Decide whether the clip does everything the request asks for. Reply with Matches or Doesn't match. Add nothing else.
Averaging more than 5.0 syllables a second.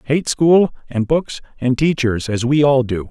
Doesn't match